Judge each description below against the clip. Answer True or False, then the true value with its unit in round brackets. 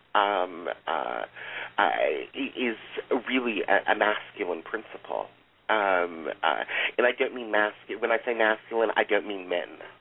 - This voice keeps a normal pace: True (150 wpm)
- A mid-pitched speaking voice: False (120 Hz)